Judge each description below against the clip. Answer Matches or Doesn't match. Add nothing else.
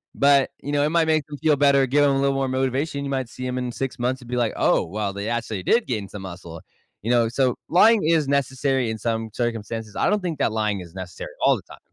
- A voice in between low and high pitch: Doesn't match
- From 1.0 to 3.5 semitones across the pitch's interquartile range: Doesn't match